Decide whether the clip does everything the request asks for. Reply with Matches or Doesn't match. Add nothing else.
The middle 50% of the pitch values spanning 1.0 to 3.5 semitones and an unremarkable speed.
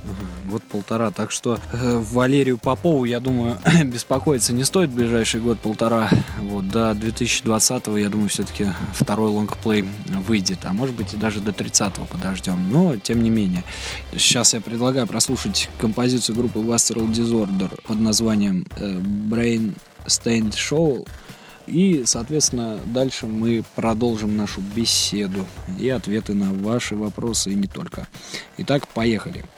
Matches